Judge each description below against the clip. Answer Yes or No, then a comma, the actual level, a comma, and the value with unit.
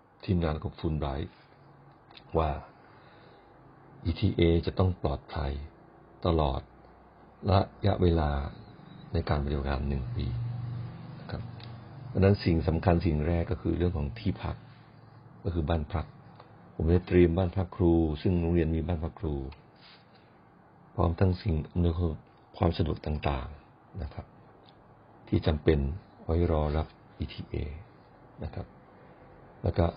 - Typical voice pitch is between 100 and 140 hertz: No, very low, 85 Hz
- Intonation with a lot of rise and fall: No, average, 3.7 semitones